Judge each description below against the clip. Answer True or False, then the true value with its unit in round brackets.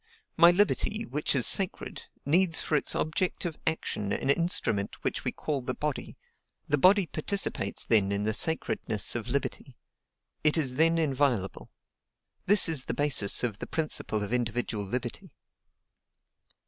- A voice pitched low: False (145 Hz)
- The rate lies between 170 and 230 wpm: False (145 wpm)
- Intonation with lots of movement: True (6.0 semitones)